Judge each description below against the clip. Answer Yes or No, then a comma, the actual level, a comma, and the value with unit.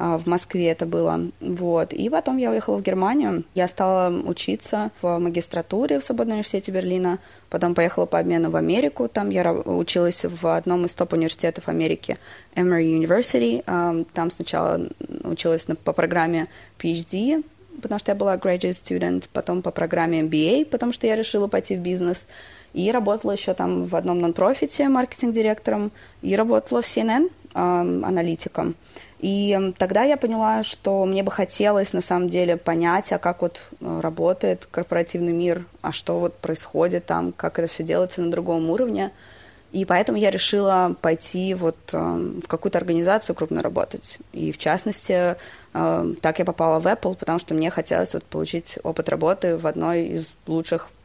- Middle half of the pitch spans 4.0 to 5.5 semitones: No, average, 3.1 semitones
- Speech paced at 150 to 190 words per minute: Yes, average, 155 wpm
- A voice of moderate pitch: Yes, medium, 175 Hz